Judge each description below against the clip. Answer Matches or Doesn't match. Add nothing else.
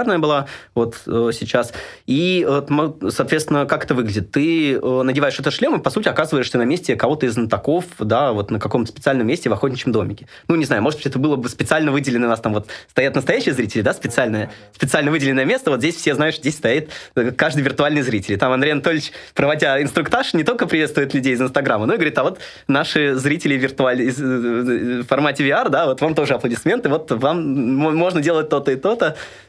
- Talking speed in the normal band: Doesn't match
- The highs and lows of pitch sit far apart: Doesn't match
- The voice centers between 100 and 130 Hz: Doesn't match